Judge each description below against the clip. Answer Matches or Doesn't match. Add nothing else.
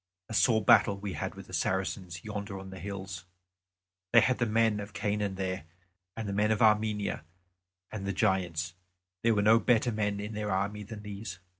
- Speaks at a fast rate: Doesn't match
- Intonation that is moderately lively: Doesn't match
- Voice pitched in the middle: Doesn't match